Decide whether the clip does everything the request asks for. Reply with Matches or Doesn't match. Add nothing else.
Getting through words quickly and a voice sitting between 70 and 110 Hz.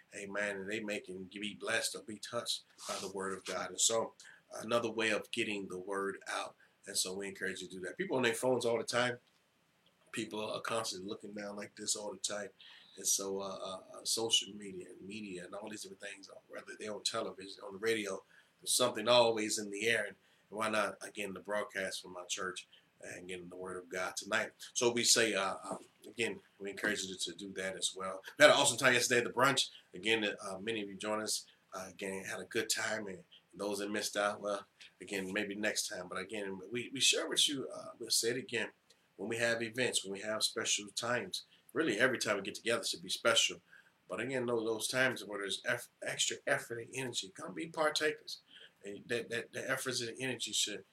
Matches